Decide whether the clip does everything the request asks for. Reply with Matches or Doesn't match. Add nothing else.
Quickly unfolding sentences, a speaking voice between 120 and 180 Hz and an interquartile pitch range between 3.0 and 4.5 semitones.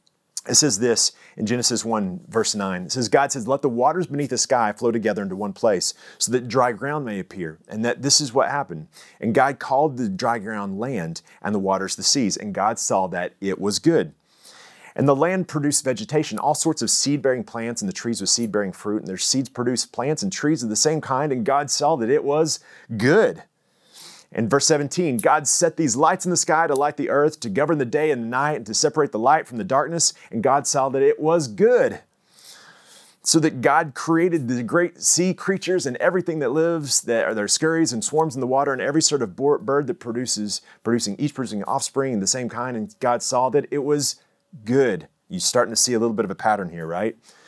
Doesn't match